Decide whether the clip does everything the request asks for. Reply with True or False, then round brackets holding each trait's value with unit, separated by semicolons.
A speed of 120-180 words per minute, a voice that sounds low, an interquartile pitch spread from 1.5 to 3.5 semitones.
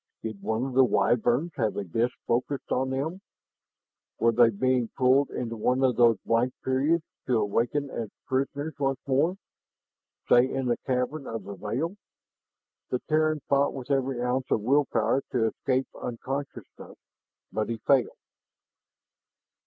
True (150 wpm; 130 Hz; 2.9 semitones)